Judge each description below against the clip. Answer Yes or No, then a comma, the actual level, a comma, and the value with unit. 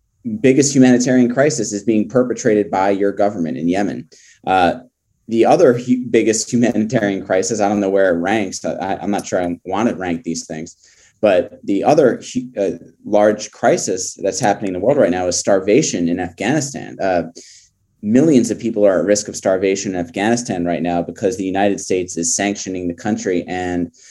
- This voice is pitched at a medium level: No, low, 100 Hz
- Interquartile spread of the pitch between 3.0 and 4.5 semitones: Yes, average, 4.0 semitones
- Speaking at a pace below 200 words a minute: Yes, average, 185 wpm